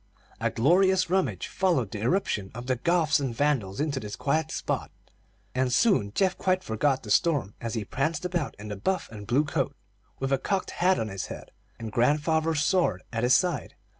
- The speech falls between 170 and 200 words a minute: Yes, average, 195 wpm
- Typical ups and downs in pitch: No, wide, 7.1 semitones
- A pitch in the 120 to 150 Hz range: Yes, medium, 140 Hz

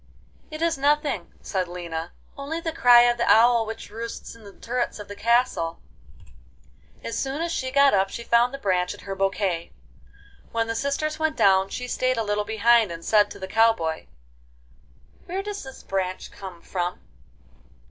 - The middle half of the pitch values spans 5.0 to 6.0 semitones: Yes, wide, 5.5 semitones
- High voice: Yes, high, 225 Hz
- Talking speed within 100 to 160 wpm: No, average, 185 wpm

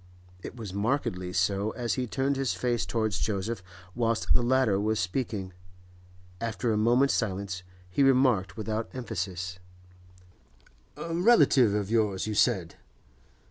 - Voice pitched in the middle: No, low, 110 Hz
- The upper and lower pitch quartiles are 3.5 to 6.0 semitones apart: Yes, average, 4.1 semitones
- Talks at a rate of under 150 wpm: Yes, slow, 135 wpm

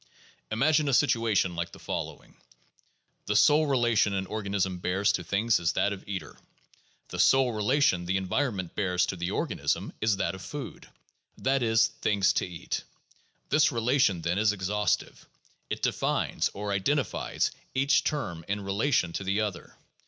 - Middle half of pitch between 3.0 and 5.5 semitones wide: Yes, average, 4.8 semitones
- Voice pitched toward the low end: Yes, low, 105 Hz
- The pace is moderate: Yes, average, 160 wpm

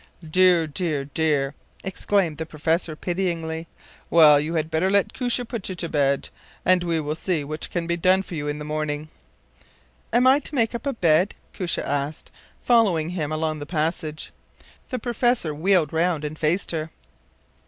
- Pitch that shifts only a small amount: No, average, 3.4 semitones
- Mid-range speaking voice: Yes, medium, 165 Hz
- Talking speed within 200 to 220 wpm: No, average, 175 wpm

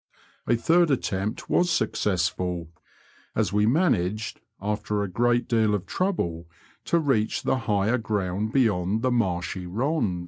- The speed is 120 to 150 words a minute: Yes, slow, 135 wpm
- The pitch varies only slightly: No, average, 4.5 semitones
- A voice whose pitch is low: Yes, low, 105 Hz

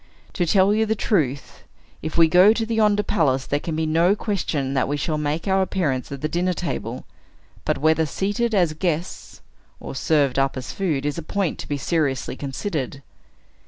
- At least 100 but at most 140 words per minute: No, average, 190 wpm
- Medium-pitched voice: Yes, medium, 160 Hz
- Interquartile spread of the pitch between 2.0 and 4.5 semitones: No, average, 5.2 semitones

